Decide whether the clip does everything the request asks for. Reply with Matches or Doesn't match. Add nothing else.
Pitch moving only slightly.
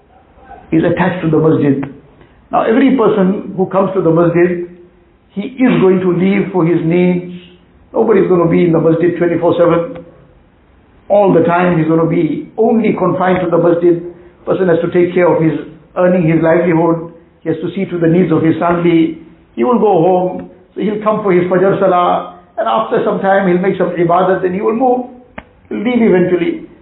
Matches